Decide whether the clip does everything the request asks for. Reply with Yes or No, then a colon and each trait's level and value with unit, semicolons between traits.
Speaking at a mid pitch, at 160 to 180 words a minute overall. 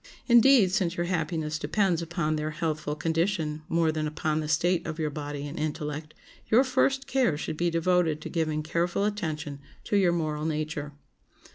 Yes: medium, 160 Hz; average, 170 wpm